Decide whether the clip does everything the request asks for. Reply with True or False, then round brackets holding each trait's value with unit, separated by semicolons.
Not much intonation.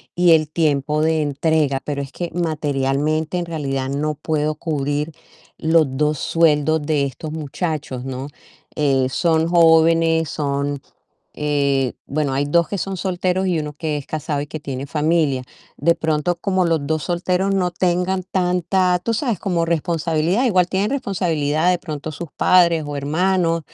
False (3.1 semitones)